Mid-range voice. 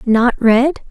No: high, 245 Hz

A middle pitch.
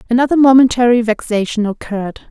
No: high, 235 Hz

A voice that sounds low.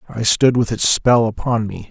Yes: low, 115 Hz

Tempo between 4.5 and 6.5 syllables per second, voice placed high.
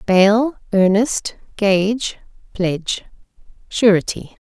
No: 3.1 syllables/s; high, 205 Hz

